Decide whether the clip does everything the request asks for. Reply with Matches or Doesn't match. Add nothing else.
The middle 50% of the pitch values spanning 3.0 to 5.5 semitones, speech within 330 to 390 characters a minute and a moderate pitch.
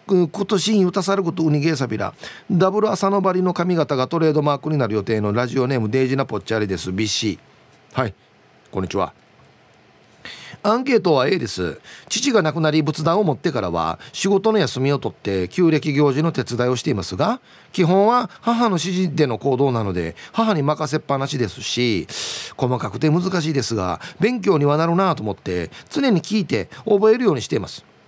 Doesn't match